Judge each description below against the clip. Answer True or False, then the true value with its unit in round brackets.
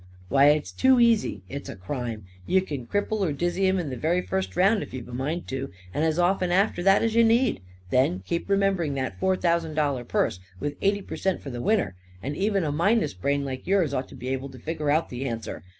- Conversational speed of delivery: False (235 wpm)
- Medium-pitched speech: True (160 Hz)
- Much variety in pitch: True (6.4 semitones)